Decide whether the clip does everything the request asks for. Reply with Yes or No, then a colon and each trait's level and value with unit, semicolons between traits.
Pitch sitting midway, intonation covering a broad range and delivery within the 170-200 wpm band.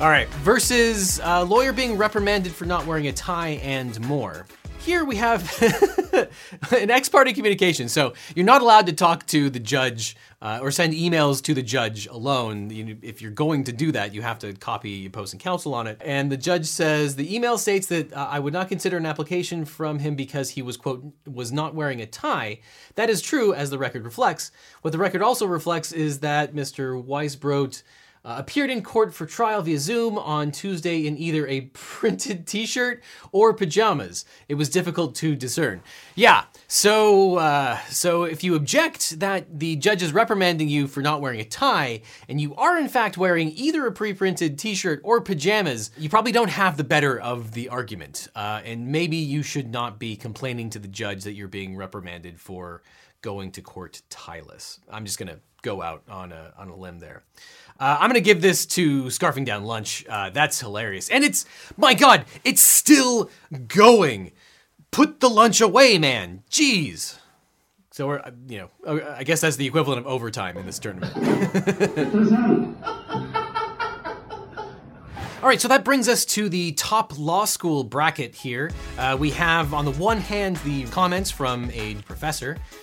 Yes: medium, 155 Hz; wide, 7.8 semitones; average, 185 wpm